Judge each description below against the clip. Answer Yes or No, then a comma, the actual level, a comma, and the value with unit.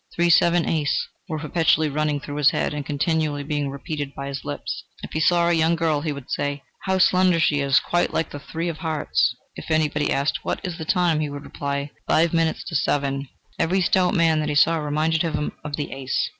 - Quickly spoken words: Yes, fast, 220 wpm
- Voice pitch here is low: No, medium, 155 Hz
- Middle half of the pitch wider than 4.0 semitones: No, narrow, 2.5 semitones